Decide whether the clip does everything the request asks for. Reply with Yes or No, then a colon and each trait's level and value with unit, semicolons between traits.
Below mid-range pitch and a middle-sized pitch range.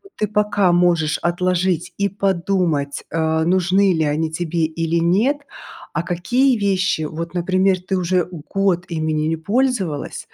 No: medium, 175 Hz; average, 3.1 semitones